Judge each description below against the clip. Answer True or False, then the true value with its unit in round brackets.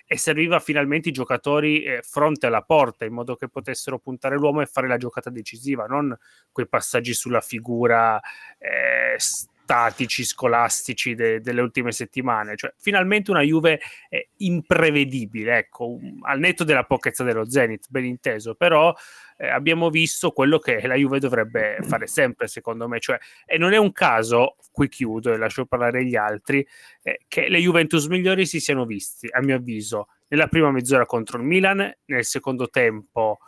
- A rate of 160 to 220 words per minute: True (170 wpm)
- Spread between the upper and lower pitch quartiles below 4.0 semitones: False (4.8 semitones)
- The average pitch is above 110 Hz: True (130 Hz)